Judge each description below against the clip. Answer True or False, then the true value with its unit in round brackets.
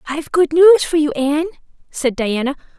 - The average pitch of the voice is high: True (305 Hz)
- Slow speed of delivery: False (170 wpm)